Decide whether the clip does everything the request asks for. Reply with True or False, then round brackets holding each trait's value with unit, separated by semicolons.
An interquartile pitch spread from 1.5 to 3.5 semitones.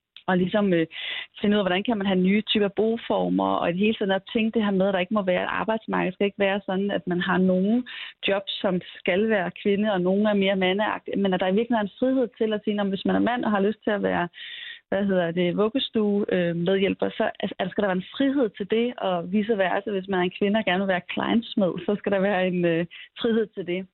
True (2.9 semitones)